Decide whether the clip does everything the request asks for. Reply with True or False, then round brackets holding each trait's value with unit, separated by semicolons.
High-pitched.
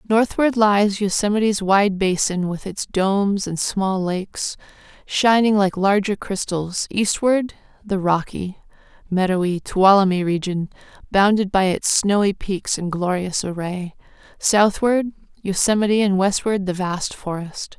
True (195 Hz)